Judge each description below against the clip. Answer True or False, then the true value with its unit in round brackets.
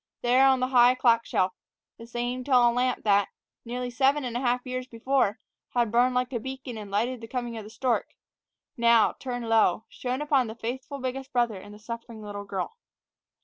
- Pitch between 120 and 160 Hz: False (245 Hz)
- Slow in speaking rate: False (195 wpm)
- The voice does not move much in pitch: True (2.1 semitones)